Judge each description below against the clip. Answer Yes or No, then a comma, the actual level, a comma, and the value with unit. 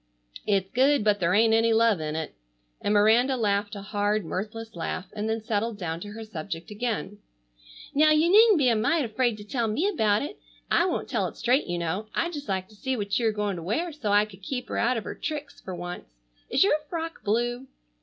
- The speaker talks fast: Yes, fast, 230 wpm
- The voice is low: No, high, 215 Hz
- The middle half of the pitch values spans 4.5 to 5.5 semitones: No, average, 3.9 semitones